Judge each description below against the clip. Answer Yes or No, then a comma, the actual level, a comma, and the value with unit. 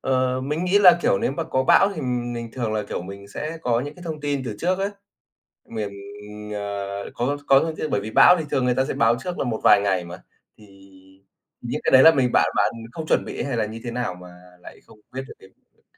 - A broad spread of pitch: Yes, wide, 5.7 semitones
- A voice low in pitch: Yes, low, 130 Hz